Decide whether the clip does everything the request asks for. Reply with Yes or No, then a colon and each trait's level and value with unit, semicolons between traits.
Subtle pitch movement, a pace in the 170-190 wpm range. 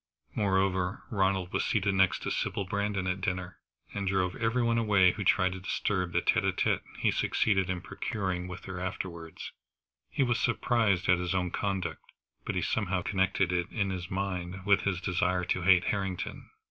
Yes: narrow, 1.7 semitones; average, 185 wpm